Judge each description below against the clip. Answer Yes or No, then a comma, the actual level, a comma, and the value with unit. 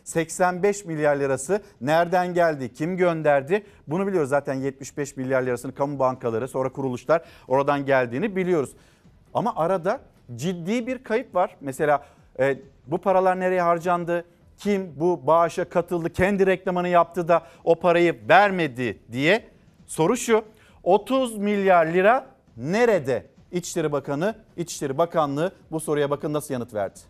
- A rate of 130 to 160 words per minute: Yes, average, 135 wpm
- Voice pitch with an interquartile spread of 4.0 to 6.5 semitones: Yes, average, 4.6 semitones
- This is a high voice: No, medium, 170 Hz